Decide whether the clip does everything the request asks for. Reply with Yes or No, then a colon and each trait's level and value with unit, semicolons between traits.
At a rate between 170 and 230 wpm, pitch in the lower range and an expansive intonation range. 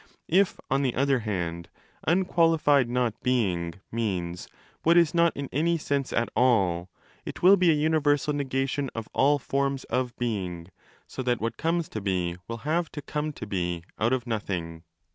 Yes: average, 180 wpm; low, 125 Hz; wide, 6.6 semitones